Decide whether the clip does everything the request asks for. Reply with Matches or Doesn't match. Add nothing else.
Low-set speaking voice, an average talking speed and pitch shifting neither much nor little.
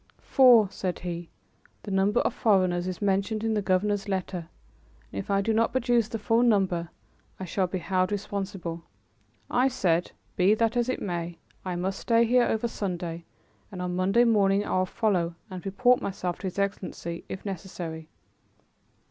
Doesn't match